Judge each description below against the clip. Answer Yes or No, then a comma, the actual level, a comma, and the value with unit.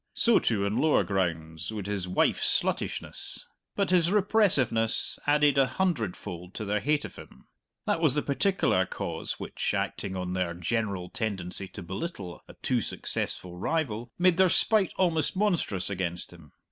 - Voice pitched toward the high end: No, low, 110 Hz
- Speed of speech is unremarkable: Yes, average, 160 wpm